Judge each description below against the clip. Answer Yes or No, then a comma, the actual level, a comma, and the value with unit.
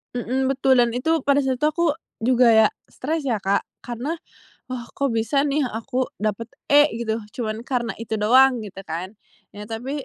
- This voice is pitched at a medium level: No, high, 245 Hz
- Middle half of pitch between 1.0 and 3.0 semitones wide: No, average, 3.5 semitones